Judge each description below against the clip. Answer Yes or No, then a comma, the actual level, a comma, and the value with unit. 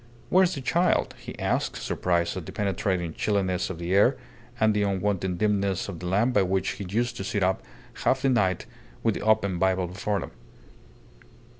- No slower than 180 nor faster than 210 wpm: Yes, average, 190 wpm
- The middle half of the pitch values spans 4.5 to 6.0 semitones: No, narrow, 2.6 semitones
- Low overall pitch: Yes, low, 100 Hz